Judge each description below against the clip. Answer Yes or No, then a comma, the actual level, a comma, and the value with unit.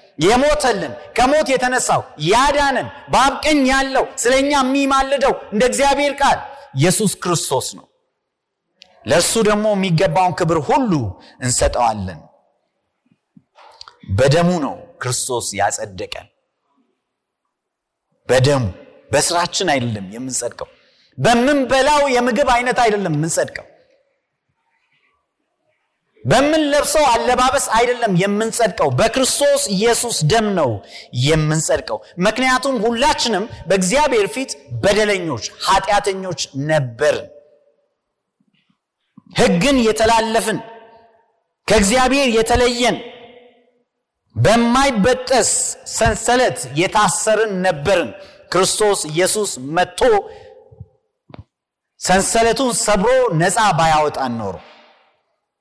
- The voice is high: Yes, high, 225 Hz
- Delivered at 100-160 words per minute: No, slow, 70 wpm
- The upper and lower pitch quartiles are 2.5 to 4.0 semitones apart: No, wide, 7.1 semitones